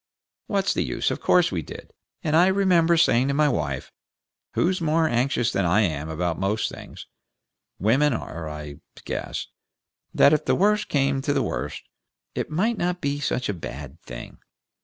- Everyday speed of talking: Yes, average, 175 wpm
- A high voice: No, low, 135 Hz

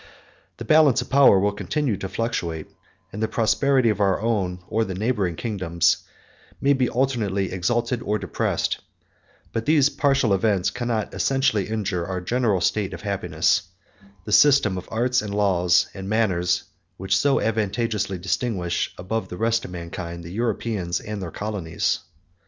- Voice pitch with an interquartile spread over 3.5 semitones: Yes, average, 4.1 semitones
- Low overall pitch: Yes, low, 105 Hz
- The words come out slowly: No, average, 155 wpm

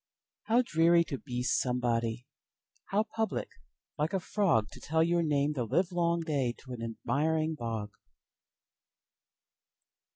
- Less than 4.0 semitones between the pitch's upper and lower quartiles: No, wide, 5.6 semitones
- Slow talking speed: Yes, slow, 105 wpm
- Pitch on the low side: No, medium, 150 Hz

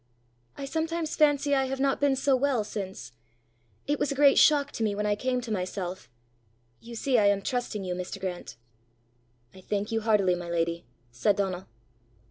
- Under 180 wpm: No, average, 185 wpm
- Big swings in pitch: Yes, wide, 6.4 semitones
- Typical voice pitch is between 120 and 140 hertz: No, high, 215 Hz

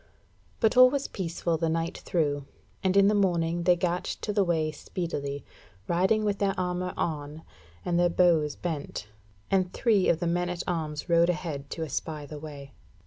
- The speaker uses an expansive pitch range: No, average, 2.9 semitones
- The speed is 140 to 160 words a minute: No, average, 180 wpm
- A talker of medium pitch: Yes, medium, 170 Hz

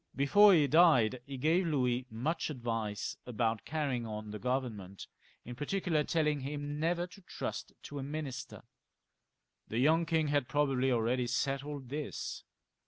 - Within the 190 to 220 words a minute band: No, average, 150 wpm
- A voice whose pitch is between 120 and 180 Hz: Yes, medium, 140 Hz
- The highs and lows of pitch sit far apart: No, average, 4.1 semitones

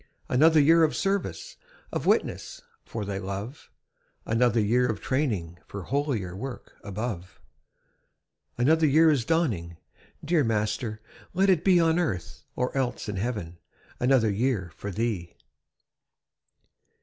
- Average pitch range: No, wide, 7.1 semitones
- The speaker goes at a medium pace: No, slow, 125 wpm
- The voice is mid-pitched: No, low, 120 Hz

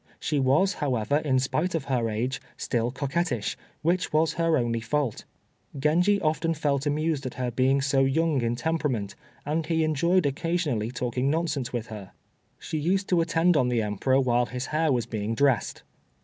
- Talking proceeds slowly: No, average, 175 wpm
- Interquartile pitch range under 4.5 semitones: No, average, 4.8 semitones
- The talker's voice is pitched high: No, medium, 140 Hz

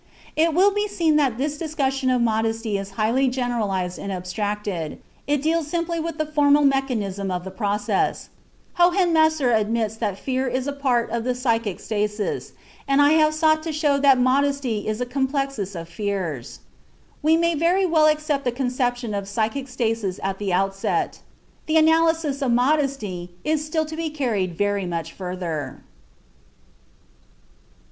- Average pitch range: No, wide, 6.8 semitones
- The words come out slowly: No, average, 155 wpm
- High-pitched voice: Yes, very high, 250 Hz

